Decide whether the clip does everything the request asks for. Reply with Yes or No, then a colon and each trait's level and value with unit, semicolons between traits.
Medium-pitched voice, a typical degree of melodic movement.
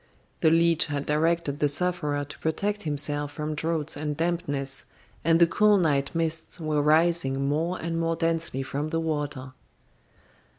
No: medium, 155 Hz; narrow, 2.3 semitones